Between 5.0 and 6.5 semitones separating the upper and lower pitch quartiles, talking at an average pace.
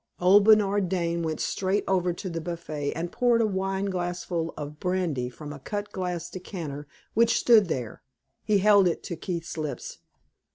No: average, 3.2 semitones; average, 170 wpm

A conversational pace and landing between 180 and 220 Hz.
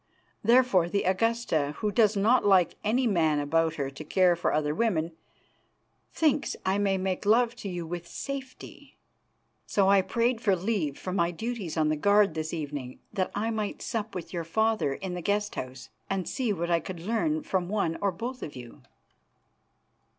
Yes: average, 180 wpm; high, 190 Hz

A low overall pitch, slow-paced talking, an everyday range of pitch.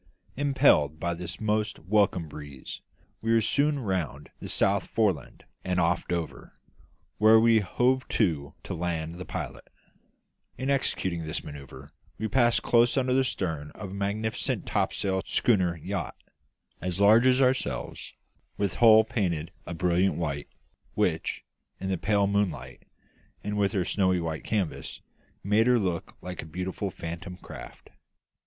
No: very low, 95 Hz; average, 145 wpm; average, 4.5 semitones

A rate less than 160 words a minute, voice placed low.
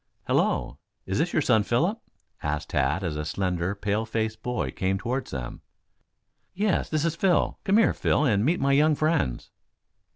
No: average, 170 wpm; low, 110 Hz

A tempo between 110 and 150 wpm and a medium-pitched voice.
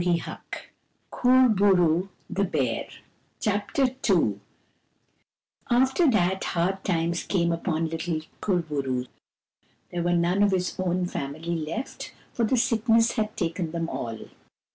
Yes: slow, 135 wpm; medium, 180 Hz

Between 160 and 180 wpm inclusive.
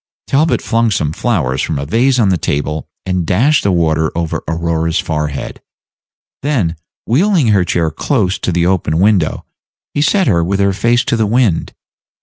Yes: average, 170 wpm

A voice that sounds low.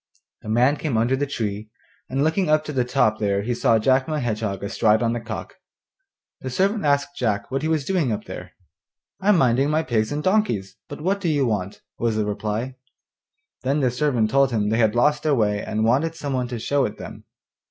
Yes: low, 125 Hz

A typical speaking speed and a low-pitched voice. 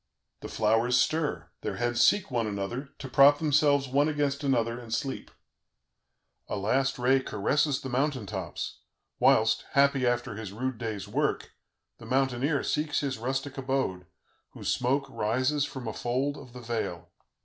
Yes: average, 155 wpm; low, 130 Hz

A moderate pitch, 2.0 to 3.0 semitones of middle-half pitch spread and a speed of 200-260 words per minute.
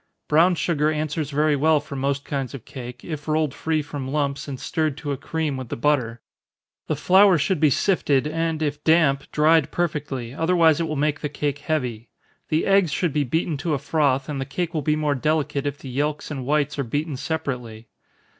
Yes: medium, 150 Hz; narrow, 2.4 semitones; fast, 205 wpm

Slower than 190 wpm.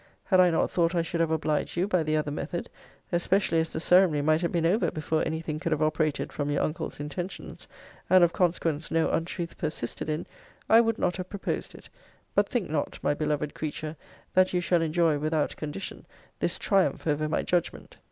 No: average, 200 wpm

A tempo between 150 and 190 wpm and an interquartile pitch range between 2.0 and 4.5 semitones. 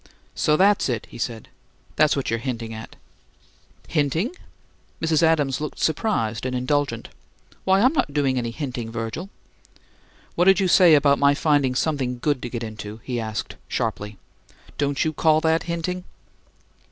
No: average, 155 wpm; average, 5.3 semitones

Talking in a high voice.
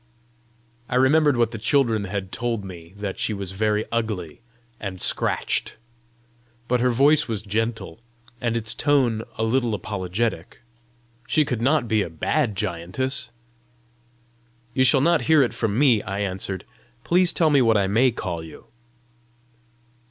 No: low, 115 Hz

